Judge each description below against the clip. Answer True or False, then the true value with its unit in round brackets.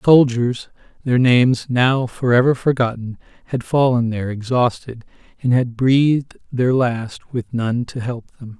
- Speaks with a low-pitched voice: True (125 Hz)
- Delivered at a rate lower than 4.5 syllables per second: True (4.3 syllables/s)